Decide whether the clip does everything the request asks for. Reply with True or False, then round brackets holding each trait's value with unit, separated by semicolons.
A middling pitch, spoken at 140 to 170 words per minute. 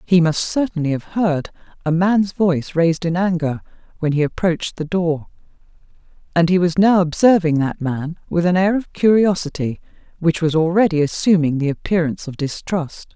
True (170 Hz; 160 wpm)